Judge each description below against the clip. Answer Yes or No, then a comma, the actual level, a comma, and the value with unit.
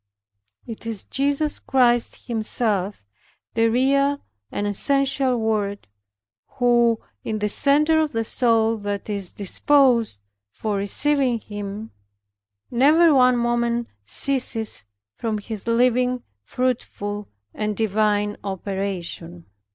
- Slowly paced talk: Yes, slow, 105 wpm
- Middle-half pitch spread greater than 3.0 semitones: Yes, average, 3.7 semitones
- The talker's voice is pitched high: Yes, high, 230 Hz